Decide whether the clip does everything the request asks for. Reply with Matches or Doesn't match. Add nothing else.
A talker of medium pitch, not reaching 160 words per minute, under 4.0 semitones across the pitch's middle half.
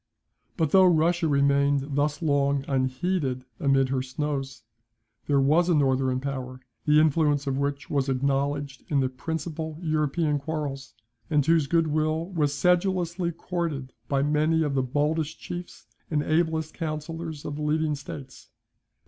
Matches